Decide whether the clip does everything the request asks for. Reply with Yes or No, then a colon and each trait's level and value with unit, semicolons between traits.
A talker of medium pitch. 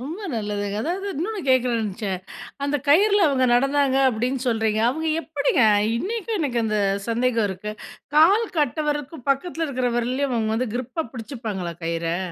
No: very high, 255 Hz